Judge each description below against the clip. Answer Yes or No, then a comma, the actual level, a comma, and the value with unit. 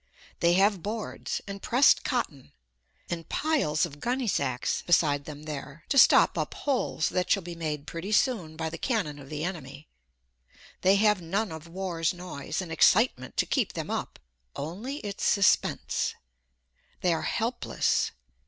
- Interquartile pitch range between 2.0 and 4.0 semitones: No, average, 5.3 semitones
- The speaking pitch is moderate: Yes, medium, 175 Hz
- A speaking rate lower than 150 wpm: No, average, 155 wpm